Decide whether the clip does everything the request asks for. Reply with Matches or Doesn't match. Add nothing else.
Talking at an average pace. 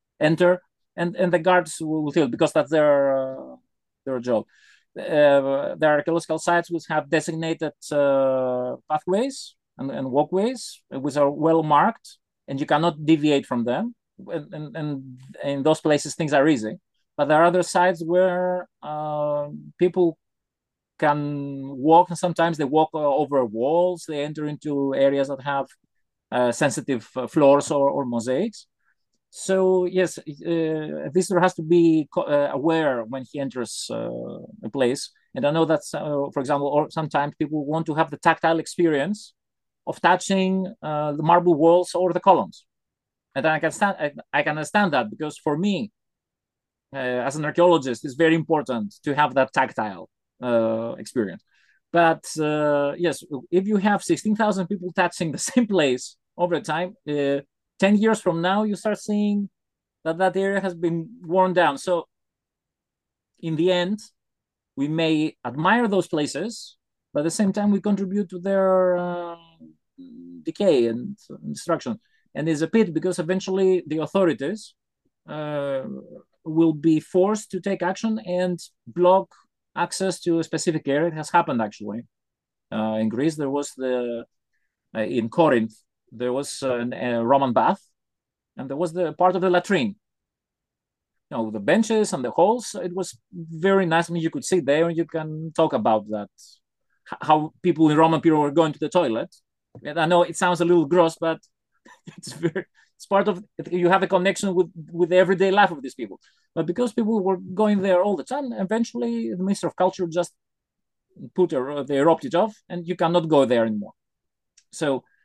Matches